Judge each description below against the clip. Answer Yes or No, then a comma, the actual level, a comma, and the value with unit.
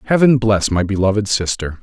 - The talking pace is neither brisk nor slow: Yes, average, 165 wpm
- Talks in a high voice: No, low, 105 Hz